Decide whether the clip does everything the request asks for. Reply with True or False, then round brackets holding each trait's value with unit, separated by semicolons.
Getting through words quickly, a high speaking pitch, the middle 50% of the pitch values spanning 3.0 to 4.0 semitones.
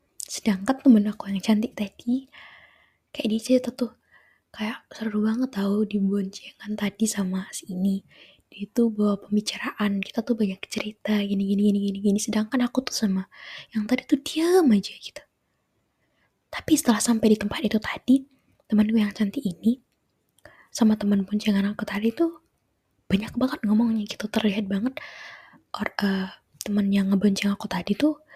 True (155 wpm; 215 Hz; 3.3 semitones)